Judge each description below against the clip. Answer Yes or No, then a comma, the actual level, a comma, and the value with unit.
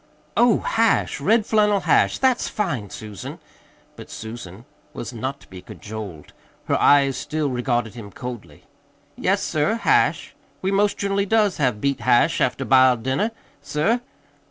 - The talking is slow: No, average, 145 wpm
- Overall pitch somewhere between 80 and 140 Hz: Yes, low, 135 Hz